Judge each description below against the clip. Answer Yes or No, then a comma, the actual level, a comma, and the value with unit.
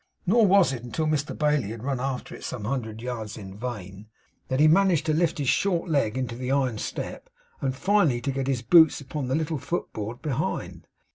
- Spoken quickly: Yes, fast, 210 wpm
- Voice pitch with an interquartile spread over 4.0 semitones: Yes, average, 4.6 semitones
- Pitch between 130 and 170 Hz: Yes, low, 135 Hz